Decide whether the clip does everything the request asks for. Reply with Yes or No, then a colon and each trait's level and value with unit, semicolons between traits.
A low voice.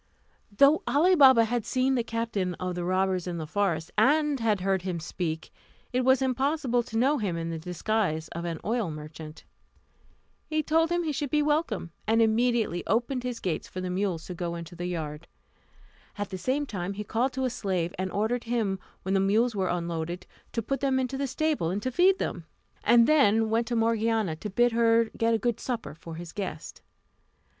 No: high, 220 Hz